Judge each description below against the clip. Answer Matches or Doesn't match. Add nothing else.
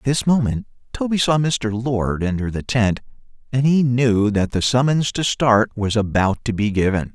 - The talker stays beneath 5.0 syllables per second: Matches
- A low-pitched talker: Matches